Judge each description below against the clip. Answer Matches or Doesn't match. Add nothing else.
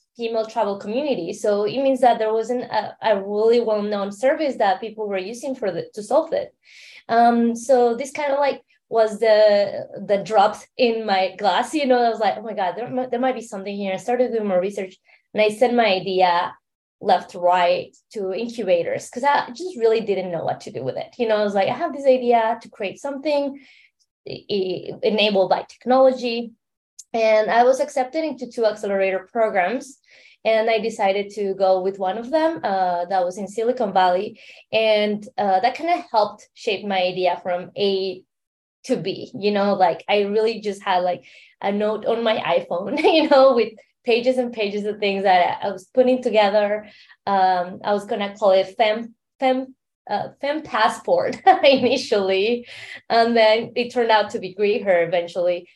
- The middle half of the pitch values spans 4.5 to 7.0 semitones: Doesn't match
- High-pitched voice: Matches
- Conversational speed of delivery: Matches